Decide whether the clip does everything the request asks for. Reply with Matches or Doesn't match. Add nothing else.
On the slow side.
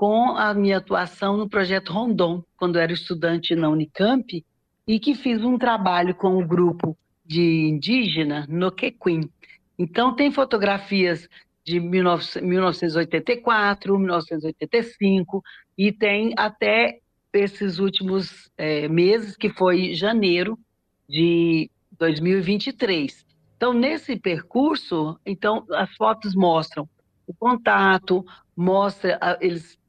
Matches